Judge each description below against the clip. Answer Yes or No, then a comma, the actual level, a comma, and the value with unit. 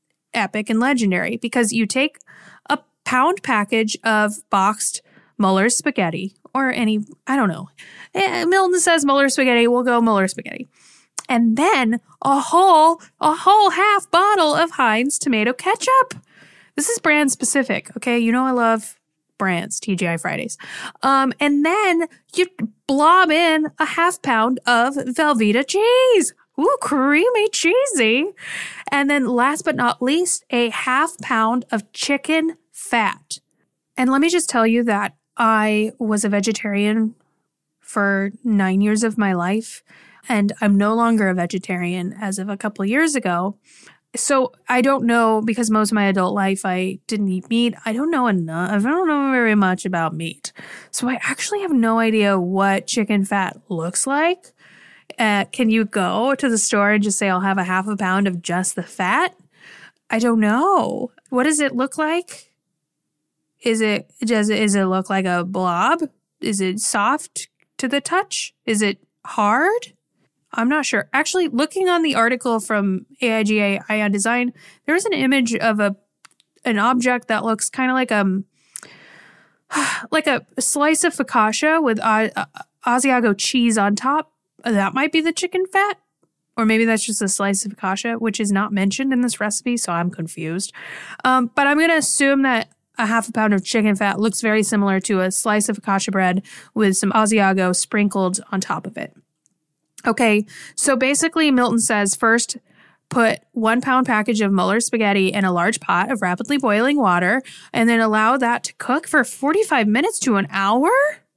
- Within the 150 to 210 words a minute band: Yes, average, 170 wpm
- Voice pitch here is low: No, high, 230 Hz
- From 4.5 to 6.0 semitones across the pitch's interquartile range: Yes, average, 5.2 semitones